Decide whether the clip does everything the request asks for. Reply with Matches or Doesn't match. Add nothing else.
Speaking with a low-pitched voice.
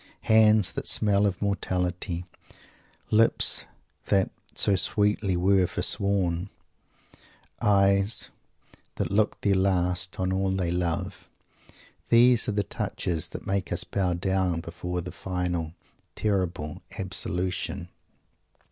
Matches